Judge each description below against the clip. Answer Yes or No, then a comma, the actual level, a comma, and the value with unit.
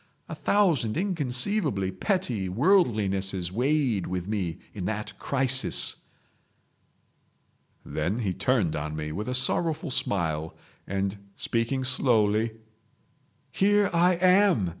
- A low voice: Yes, low, 115 Hz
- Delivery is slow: Yes, slow, 105 wpm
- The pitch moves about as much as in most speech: No, wide, 7.8 semitones